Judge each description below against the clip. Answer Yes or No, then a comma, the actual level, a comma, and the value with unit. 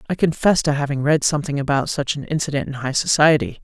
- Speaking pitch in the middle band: Yes, medium, 145 Hz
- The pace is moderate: No, fast, 215 wpm